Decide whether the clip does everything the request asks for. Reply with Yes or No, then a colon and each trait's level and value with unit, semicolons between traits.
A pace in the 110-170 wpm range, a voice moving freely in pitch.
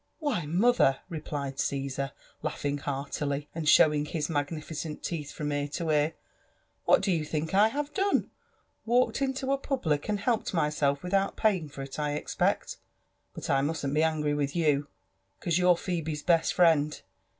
No: average, 160 wpm; average, 3.8 semitones